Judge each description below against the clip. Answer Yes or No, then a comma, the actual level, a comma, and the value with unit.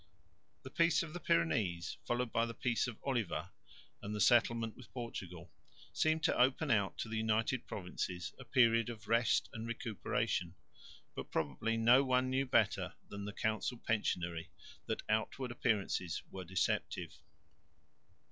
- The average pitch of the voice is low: Yes, low, 115 Hz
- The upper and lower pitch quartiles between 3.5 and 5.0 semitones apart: Yes, average, 4.4 semitones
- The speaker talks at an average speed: Yes, average, 145 wpm